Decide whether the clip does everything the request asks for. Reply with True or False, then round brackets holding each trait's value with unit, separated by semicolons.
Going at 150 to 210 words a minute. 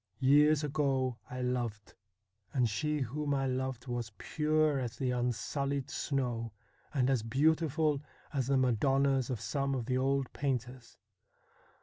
False (135 wpm)